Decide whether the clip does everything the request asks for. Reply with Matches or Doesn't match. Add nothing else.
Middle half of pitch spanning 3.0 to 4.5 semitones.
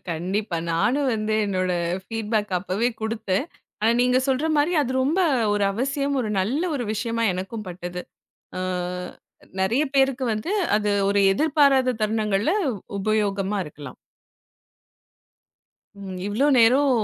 Doesn't match